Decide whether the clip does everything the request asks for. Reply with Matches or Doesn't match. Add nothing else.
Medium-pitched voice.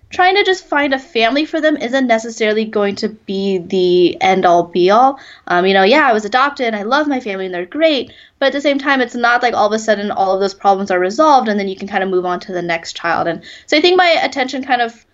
Doesn't match